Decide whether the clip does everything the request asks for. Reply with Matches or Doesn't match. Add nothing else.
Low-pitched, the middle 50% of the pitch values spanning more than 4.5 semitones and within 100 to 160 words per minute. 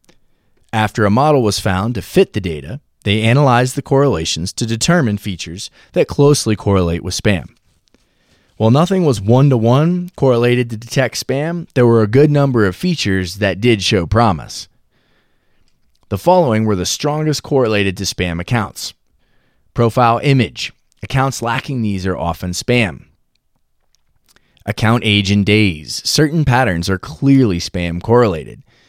Matches